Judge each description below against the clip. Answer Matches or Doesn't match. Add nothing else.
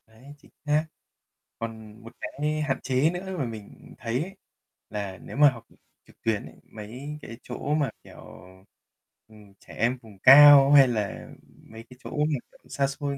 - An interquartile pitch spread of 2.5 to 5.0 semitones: Matches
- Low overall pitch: Matches